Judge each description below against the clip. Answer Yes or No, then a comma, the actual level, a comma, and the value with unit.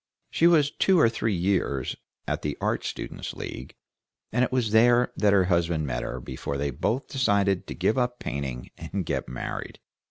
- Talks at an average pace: Yes, average, 185 wpm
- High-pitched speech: No, low, 100 Hz